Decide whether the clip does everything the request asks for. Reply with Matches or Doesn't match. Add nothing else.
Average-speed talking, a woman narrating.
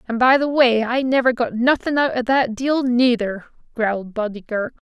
Matches